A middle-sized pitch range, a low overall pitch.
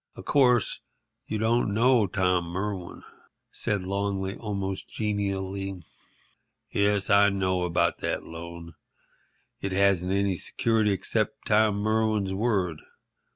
No: narrow, 2.2 semitones; low, 100 Hz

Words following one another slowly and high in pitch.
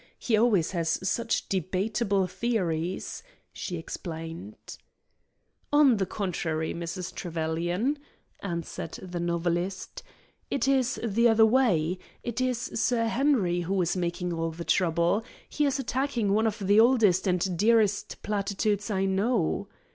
Yes: slow, 130 wpm; high, 195 Hz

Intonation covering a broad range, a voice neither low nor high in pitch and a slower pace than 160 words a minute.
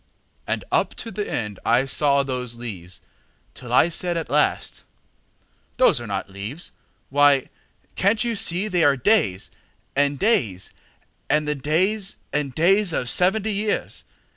Yes: wide, 7.7 semitones; medium, 145 Hz; average, 145 wpm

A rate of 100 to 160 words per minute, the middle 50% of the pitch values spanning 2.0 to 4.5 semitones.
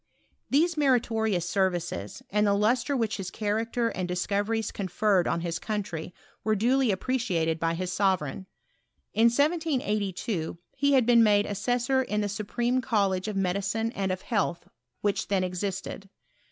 Yes: average, 140 wpm; average, 3.9 semitones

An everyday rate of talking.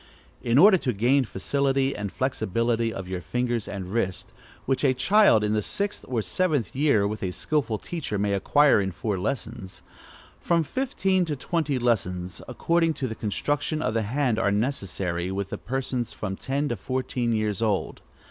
Yes: average, 170 wpm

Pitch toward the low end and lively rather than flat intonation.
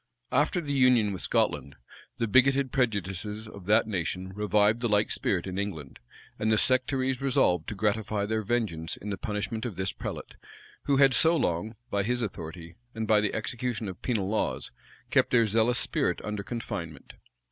No: low, 105 Hz; average, 3.7 semitones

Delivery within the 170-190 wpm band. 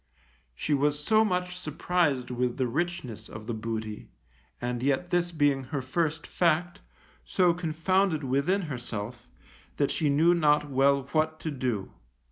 No: average, 145 wpm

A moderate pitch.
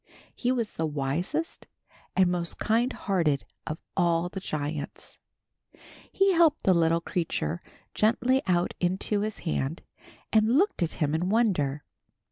Yes: medium, 180 Hz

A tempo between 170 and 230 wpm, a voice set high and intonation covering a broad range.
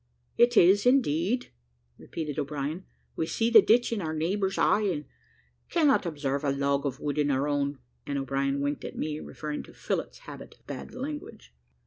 No: average, 175 wpm; medium, 155 Hz; wide, 6.6 semitones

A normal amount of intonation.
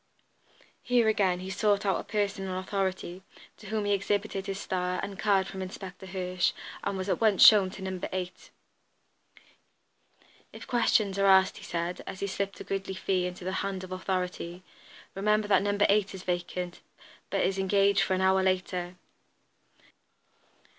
No: narrow, 1.3 semitones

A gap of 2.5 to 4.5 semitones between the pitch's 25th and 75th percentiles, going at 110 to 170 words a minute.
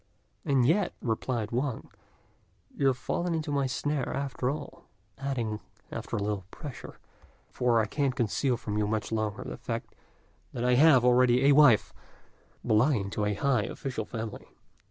Yes: average, 4.0 semitones; average, 155 wpm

